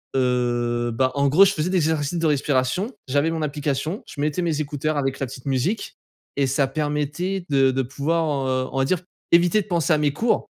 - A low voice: No, medium, 145 Hz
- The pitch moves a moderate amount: Yes, average, 3.6 semitones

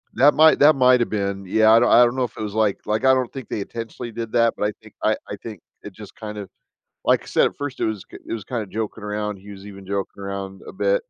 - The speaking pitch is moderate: No, low, 110 Hz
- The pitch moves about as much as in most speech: Yes, average, 3.2 semitones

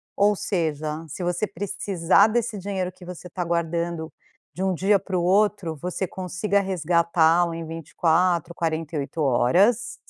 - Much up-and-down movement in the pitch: No, average, 2.8 semitones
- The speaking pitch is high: No, medium, 175 Hz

